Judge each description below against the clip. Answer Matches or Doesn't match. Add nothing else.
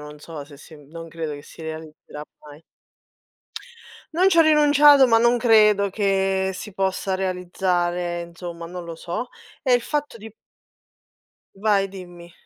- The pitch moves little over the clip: Doesn't match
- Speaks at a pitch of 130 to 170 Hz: Doesn't match